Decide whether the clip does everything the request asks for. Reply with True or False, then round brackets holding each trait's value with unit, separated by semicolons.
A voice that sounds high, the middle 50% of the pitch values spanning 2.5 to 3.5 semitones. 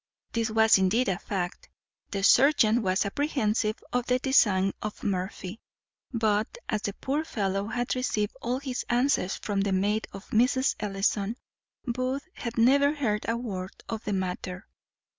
False (220 Hz; 4.0 semitones)